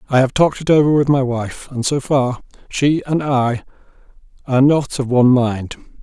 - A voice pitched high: No, low, 130 Hz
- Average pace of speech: Yes, average, 190 wpm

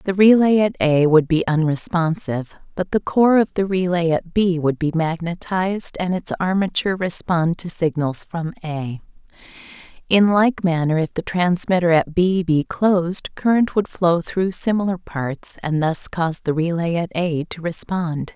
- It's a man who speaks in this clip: No, female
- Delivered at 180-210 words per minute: No, average, 165 wpm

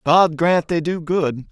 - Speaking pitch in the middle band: Yes, medium, 165 Hz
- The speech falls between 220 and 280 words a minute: No, average, 200 wpm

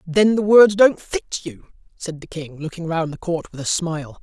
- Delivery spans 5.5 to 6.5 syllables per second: No, 4.7 syllables/s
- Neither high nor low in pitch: Yes, medium, 170 Hz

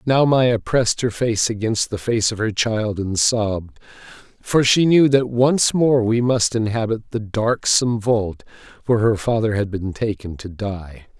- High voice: No, low, 110 Hz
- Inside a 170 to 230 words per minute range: Yes, average, 175 wpm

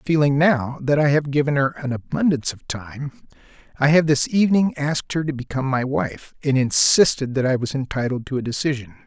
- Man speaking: Yes, male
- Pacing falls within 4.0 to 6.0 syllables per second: Yes, 5.7 syllables/s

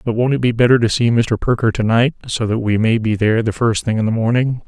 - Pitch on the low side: Yes, low, 115 Hz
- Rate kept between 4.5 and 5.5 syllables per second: No, 6.1 syllables/s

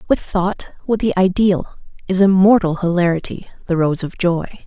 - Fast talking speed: No, average, 155 wpm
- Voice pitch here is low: No, medium, 185 Hz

